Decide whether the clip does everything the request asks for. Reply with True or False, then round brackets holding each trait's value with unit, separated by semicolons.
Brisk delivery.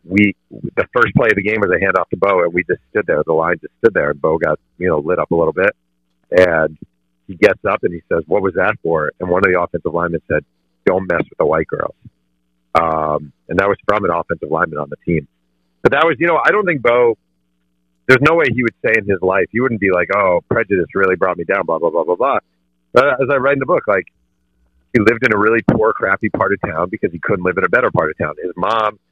True (265 wpm)